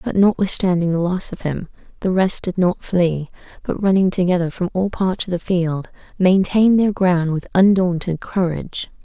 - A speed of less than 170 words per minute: No, average, 175 wpm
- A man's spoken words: No, female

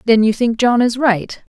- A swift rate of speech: Yes, fast, 230 wpm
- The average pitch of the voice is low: No, high, 230 Hz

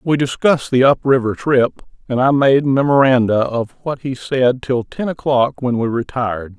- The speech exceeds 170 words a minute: Yes, average, 180 wpm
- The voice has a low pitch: Yes, low, 130 Hz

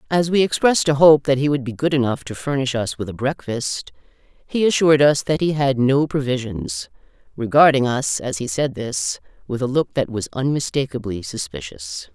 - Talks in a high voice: No, low, 135 Hz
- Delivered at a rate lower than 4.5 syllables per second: No, 5.1 syllables/s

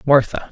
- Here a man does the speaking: Yes, male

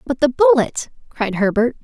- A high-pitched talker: Yes, high, 215 Hz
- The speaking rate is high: No, average, 165 wpm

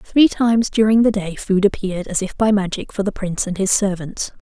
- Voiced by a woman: Yes, female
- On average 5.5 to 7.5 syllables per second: Yes, 5.6 syllables/s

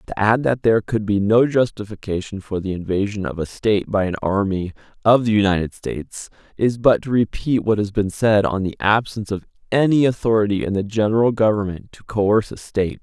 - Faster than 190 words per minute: Yes, average, 200 wpm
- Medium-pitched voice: No, low, 105 Hz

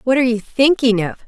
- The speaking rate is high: Yes, fast, 235 wpm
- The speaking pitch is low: No, high, 245 Hz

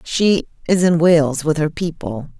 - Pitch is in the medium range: Yes, medium, 160 Hz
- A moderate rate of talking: Yes, average, 175 wpm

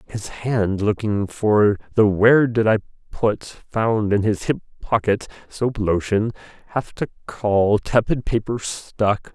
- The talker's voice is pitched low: Yes, low, 105 Hz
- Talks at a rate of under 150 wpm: Yes, average, 140 wpm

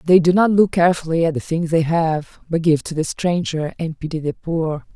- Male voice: No, female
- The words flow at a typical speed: No, fast, 230 wpm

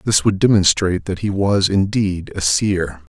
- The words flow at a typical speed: Yes, average, 170 wpm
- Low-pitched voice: Yes, very low, 95 Hz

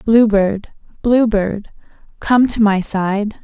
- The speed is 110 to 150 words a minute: Yes, average, 140 wpm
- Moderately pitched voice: No, high, 210 Hz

